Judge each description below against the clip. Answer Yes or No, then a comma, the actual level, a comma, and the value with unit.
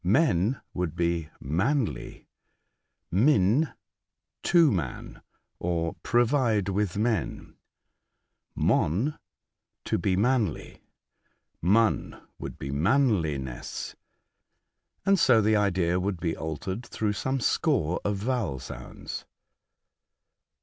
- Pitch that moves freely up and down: Yes, wide, 6.1 semitones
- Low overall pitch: Yes, low, 100 Hz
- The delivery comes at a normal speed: No, slow, 95 wpm